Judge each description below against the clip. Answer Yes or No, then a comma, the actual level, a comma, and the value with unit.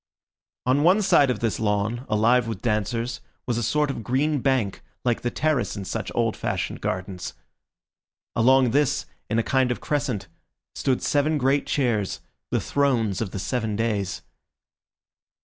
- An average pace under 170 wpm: Yes, average, 155 wpm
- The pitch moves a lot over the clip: No, average, 4.1 semitones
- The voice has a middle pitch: No, low, 120 Hz